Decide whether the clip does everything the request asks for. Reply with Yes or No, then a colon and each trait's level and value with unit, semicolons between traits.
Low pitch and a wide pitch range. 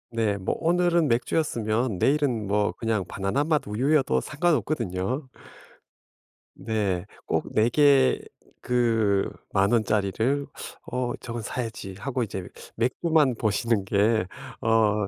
No: low, 115 Hz; average, 4.7 semitones